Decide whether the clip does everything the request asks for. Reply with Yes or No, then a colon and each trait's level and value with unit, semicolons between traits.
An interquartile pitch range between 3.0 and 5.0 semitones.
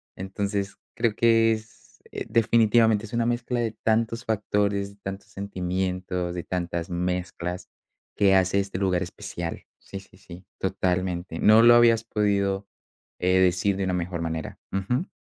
Yes: average, 3.4 semitones